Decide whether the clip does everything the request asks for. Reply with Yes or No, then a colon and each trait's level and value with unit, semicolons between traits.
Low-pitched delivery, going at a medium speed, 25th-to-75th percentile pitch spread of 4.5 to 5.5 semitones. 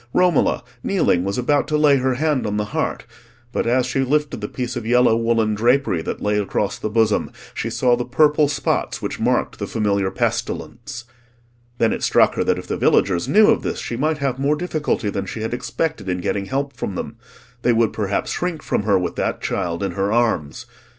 No: low, 120 Hz; fast, 210 wpm; average, 5.0 semitones